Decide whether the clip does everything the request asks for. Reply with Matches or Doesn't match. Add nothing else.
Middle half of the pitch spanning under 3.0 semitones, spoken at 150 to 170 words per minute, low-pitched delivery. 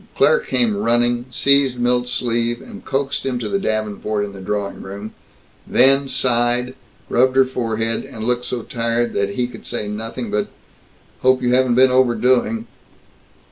Matches